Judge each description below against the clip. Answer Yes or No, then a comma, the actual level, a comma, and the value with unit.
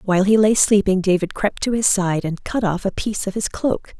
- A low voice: No, high, 200 Hz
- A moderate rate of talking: No, fast, 255 wpm